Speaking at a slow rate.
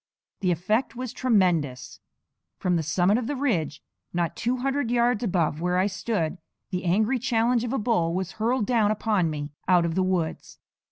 No: average, 180 wpm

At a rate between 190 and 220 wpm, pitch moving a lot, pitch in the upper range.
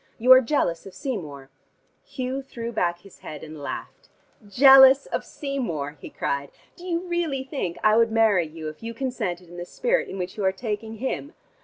Yes: average, 195 wpm; wide, 7.5 semitones; high, 225 Hz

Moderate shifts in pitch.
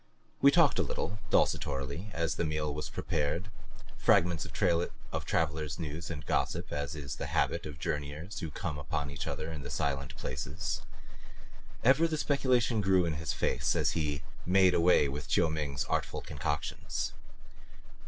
Yes: average, 4.1 semitones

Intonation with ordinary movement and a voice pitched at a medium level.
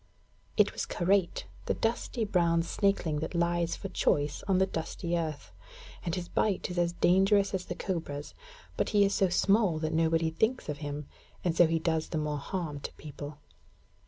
Yes: average, 3.3 semitones; medium, 170 Hz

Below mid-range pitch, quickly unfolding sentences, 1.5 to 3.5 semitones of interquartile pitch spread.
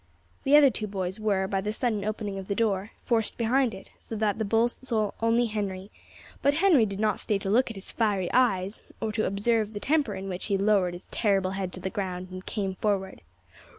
No: high, 205 Hz; fast, 220 wpm; average, 2.8 semitones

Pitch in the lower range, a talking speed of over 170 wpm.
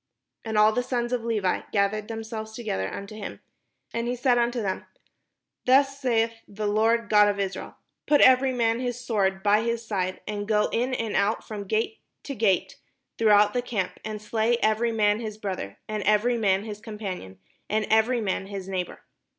No: high, 220 Hz; average, 185 wpm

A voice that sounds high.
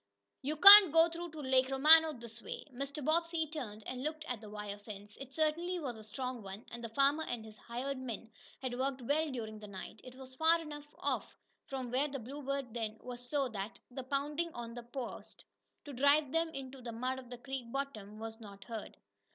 Yes: very high, 260 Hz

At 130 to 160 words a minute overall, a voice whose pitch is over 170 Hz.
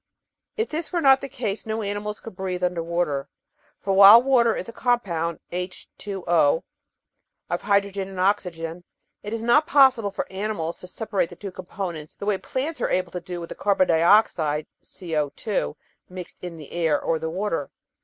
No: average, 185 wpm; high, 190 Hz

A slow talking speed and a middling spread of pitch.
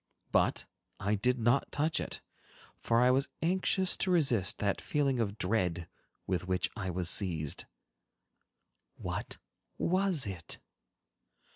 No: slow, 125 wpm; wide, 7.7 semitones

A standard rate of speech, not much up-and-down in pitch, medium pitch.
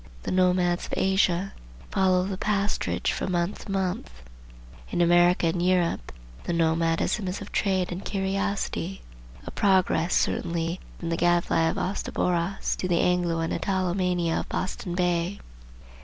Yes: average, 150 wpm; narrow, 1.8 semitones; medium, 180 Hz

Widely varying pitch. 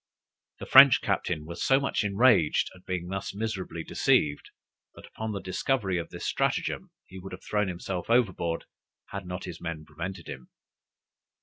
No: average, 3.3 semitones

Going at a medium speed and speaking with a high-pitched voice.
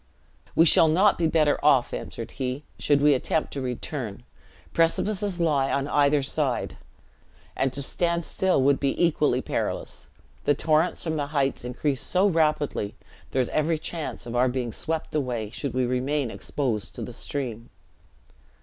No: average, 160 wpm; medium, 145 Hz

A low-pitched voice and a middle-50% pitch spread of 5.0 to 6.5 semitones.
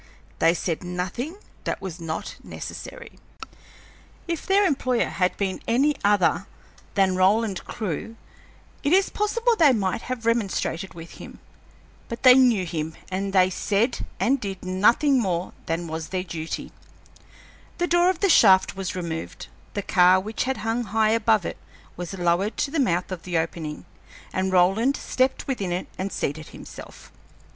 No: high, 195 Hz; wide, 5.6 semitones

